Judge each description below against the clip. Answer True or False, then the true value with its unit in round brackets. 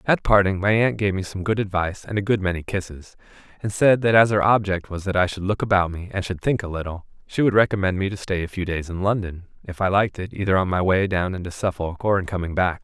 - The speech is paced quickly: True (270 wpm)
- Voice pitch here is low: True (95 Hz)